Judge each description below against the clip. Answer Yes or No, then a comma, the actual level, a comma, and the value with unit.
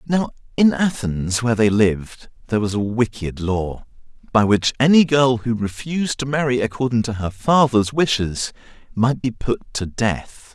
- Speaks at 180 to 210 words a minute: No, average, 165 wpm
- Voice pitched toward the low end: Yes, low, 120 Hz